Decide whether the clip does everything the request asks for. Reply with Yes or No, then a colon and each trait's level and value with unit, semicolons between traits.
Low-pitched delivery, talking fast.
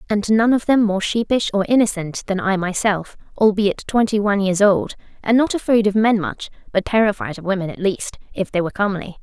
No: high, 205 Hz; fast, 210 wpm